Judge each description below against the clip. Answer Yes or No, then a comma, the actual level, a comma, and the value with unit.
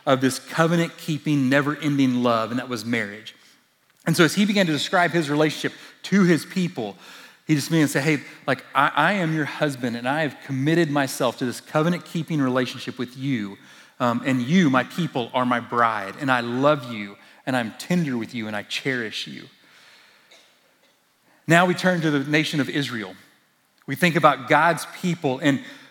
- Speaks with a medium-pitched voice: Yes, medium, 145 Hz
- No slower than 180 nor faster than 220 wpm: Yes, average, 190 wpm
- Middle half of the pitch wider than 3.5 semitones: Yes, average, 4.3 semitones